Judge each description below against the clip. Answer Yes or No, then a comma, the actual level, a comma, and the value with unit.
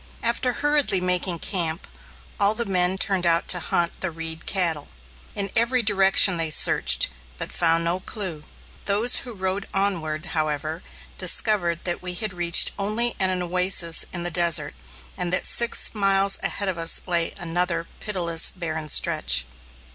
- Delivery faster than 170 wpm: No, average, 155 wpm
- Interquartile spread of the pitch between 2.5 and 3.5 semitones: Yes, average, 2.9 semitones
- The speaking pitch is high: No, medium, 180 Hz